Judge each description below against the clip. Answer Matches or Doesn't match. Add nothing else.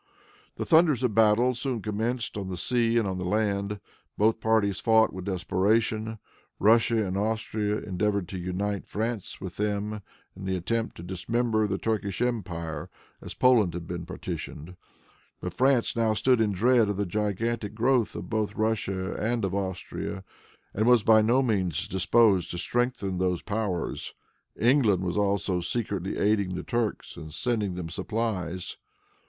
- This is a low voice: Matches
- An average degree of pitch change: Matches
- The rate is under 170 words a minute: Matches